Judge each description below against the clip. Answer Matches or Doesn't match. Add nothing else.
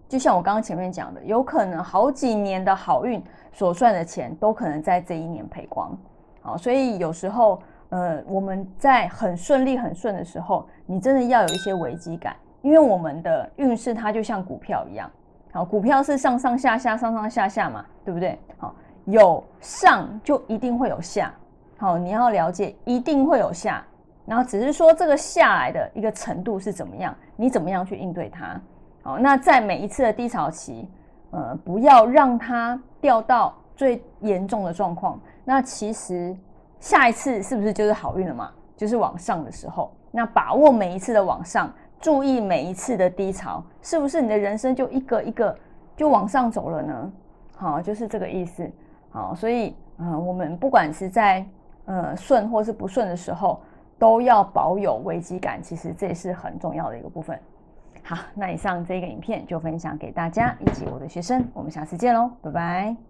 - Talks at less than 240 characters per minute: Doesn't match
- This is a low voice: Doesn't match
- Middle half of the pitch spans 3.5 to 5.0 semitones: Doesn't match